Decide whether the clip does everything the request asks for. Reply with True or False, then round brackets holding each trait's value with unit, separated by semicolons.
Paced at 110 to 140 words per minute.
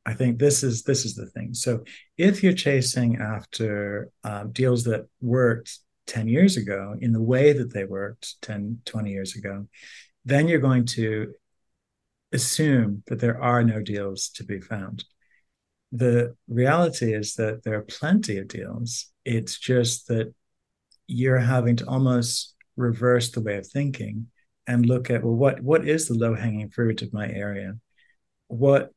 False (165 wpm)